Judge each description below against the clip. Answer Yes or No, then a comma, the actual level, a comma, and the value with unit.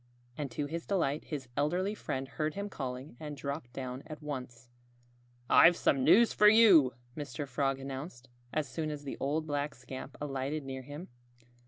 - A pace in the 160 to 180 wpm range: Yes, average, 170 wpm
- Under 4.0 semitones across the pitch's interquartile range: Yes, average, 2.9 semitones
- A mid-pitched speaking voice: Yes, medium, 145 Hz